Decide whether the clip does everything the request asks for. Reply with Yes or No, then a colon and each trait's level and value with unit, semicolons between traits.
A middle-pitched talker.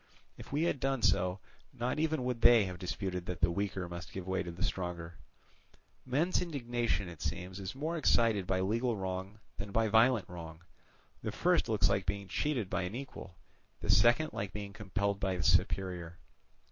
No: low, 100 Hz